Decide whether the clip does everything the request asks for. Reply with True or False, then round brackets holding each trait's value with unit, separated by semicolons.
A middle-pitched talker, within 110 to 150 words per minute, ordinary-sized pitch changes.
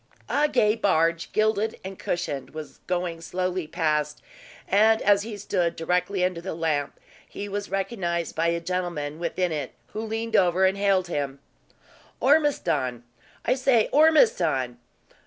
True (180 Hz; 140 wpm; 4.2 semitones)